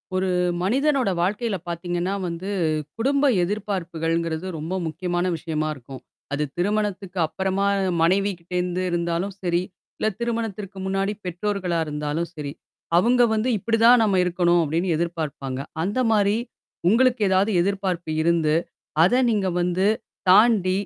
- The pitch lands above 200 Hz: No, medium, 185 Hz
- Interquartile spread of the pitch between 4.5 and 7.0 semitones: No, average, 3.5 semitones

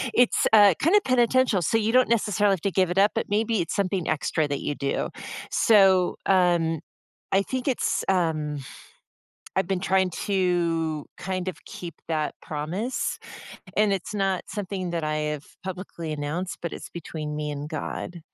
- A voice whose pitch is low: No, medium, 185 Hz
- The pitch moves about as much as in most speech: Yes, average, 4.0 semitones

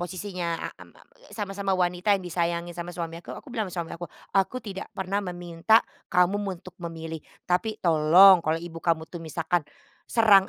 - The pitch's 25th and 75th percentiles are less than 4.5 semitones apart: Yes, narrow, 2.6 semitones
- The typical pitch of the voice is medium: Yes, medium, 175 Hz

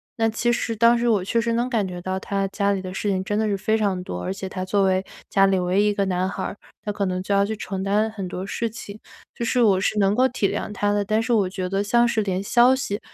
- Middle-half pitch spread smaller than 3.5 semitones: Yes, narrow, 2.6 semitones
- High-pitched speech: Yes, high, 200 Hz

